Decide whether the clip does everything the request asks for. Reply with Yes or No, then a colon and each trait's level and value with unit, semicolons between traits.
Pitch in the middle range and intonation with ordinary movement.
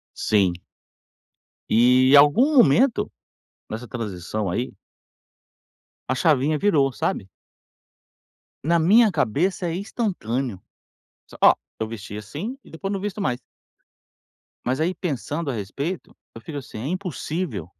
No: medium, 145 Hz; wide, 7.9 semitones